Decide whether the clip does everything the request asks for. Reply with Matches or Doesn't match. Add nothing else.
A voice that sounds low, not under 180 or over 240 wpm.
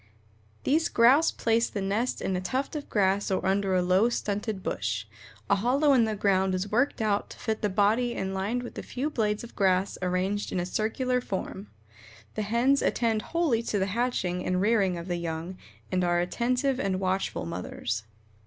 Doesn't match